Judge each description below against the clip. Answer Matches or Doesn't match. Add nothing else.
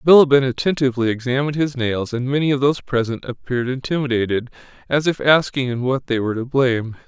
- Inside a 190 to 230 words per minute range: Doesn't match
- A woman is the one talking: Doesn't match